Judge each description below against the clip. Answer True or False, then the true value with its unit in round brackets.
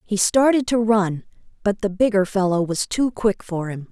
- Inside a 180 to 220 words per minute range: True (200 wpm)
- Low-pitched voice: False (205 Hz)